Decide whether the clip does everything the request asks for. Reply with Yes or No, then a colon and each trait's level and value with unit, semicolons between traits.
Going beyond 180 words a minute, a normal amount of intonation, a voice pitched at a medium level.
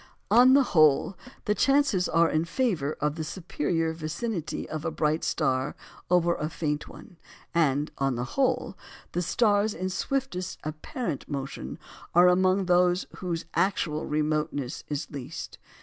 No: average, 145 wpm; average, 3.8 semitones; medium, 165 Hz